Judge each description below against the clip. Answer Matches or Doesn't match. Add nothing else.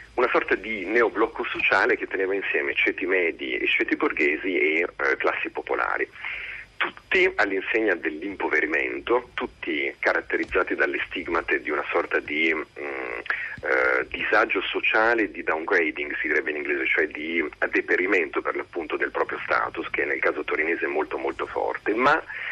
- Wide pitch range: Doesn't match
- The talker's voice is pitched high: Matches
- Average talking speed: Matches